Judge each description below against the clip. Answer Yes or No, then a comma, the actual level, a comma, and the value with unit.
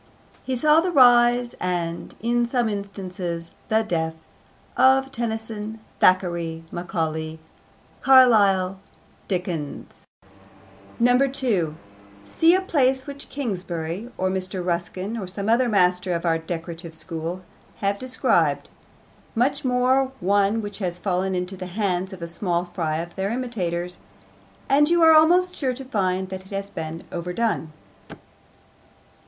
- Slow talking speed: Yes, slow, 130 wpm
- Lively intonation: Yes, wide, 5.7 semitones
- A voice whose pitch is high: Yes, high, 195 Hz